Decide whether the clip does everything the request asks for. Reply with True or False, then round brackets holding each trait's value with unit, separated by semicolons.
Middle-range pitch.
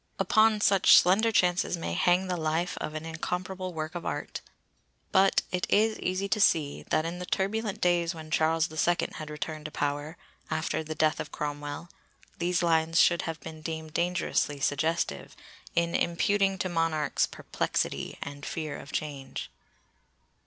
True (165 Hz)